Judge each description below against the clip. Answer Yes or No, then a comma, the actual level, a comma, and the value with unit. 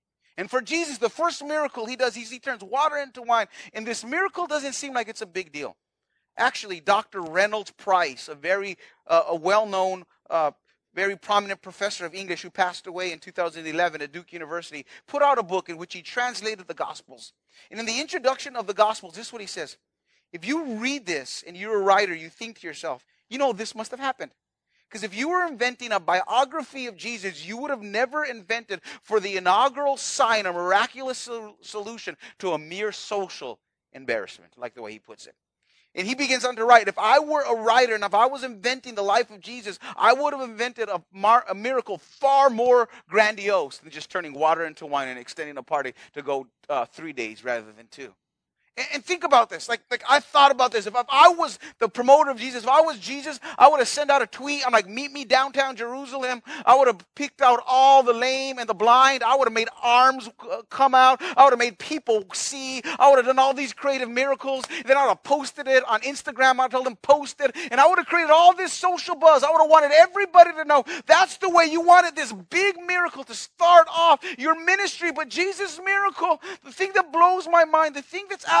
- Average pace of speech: No, fast, 225 wpm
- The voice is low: No, very high, 250 Hz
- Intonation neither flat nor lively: No, wide, 5.9 semitones